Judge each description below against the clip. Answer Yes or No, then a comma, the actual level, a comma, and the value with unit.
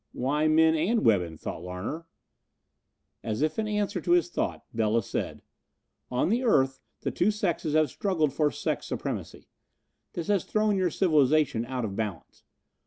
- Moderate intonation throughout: No, wide, 7.3 semitones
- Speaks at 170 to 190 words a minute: No, average, 160 wpm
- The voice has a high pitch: No, medium, 155 Hz